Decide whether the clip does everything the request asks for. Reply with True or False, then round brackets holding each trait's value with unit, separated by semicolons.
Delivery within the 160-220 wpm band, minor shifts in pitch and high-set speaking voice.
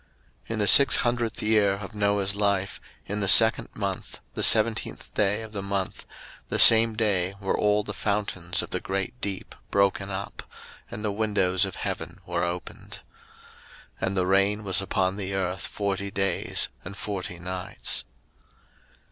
False (165 wpm; 1.6 semitones; 100 Hz)